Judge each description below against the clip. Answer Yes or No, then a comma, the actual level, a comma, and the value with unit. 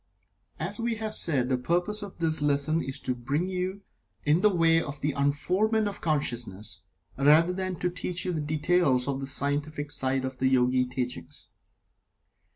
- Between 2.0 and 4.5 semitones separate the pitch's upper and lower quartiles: No, average, 5.2 semitones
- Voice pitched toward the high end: No, medium, 150 Hz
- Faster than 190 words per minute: No, average, 170 wpm